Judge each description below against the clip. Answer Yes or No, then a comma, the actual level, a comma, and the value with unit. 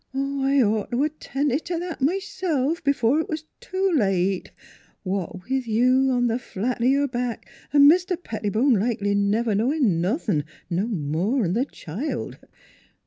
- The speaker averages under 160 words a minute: Yes, average, 150 wpm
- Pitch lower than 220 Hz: No, very high, 250 Hz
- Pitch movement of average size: No, wide, 5.7 semitones